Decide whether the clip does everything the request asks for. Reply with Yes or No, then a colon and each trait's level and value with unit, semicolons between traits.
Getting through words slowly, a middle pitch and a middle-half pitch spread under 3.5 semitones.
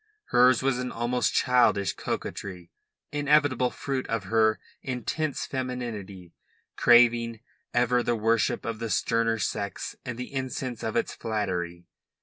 No: slow, 130 wpm; low, 120 Hz; narrow, 2.6 semitones